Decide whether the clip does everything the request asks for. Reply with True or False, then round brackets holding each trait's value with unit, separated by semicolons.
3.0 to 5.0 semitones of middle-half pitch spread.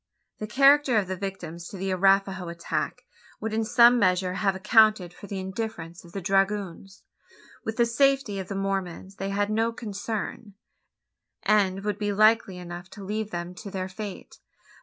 False (2.5 semitones)